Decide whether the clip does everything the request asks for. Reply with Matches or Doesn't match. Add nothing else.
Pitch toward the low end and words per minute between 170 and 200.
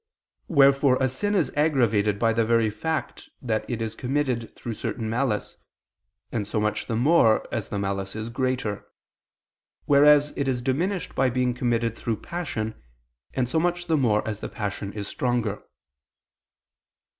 Doesn't match